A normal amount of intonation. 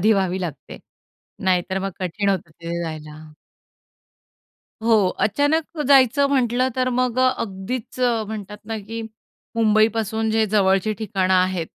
Yes: average, 3.4 semitones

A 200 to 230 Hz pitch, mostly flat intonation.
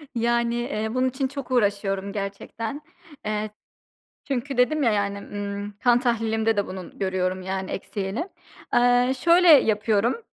No: high, 220 Hz; average, 3.7 semitones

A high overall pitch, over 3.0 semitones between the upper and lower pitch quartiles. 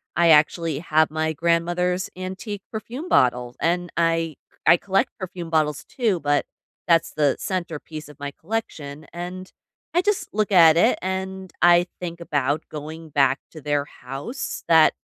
No: medium, 165 Hz; average, 3.5 semitones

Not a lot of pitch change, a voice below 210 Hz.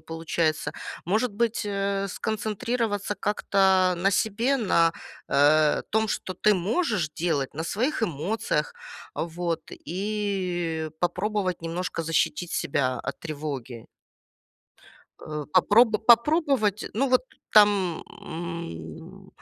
No: average, 4.6 semitones; medium, 185 Hz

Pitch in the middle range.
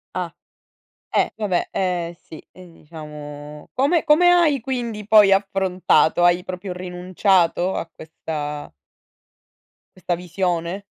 Yes: medium, 180 Hz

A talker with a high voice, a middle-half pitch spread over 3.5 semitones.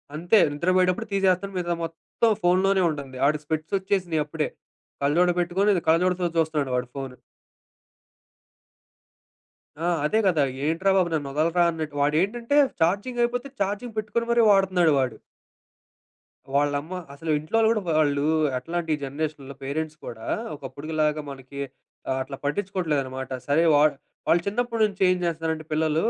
No: medium, 165 Hz; average, 4.6 semitones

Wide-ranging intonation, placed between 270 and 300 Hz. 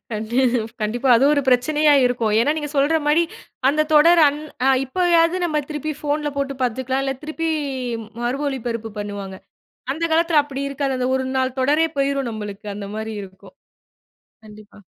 No: average, 4.5 semitones; very high, 275 Hz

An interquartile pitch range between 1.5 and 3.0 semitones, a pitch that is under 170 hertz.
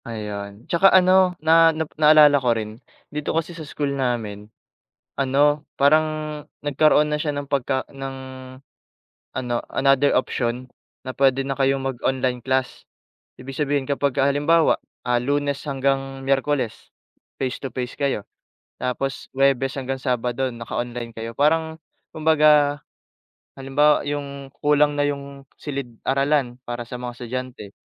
Yes: narrow, 2.6 semitones; low, 135 Hz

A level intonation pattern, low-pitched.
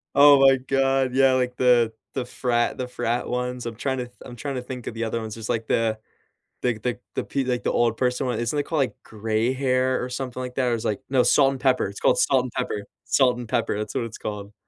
Yes: narrow, 2.1 semitones; low, 125 Hz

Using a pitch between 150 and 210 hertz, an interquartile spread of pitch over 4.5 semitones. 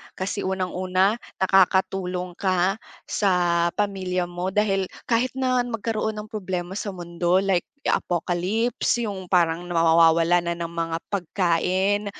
No: medium, 185 Hz; narrow, 2.6 semitones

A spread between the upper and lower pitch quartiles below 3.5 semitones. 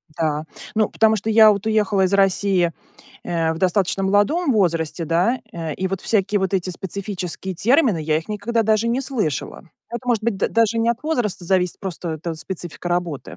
No: average, 4.2 semitones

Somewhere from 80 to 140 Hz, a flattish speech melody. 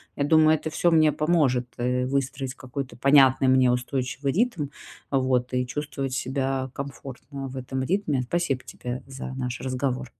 Yes: low, 135 Hz; narrow, 1.9 semitones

